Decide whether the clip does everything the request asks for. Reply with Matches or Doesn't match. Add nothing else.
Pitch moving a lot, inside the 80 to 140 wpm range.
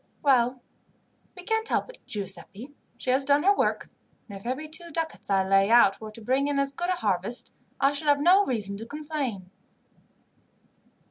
Doesn't match